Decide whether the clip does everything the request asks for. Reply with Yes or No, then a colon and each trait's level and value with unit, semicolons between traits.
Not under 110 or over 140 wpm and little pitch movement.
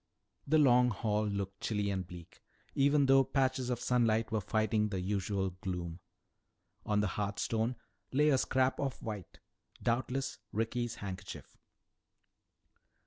No: slow, 135 wpm; average, 4.4 semitones